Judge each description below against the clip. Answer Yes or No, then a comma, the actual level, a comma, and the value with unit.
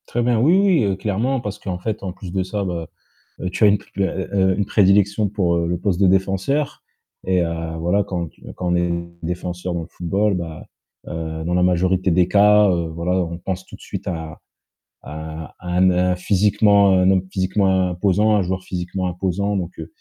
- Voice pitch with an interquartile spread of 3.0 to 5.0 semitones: No, narrow, 2.4 semitones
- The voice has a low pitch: Yes, very low, 95 Hz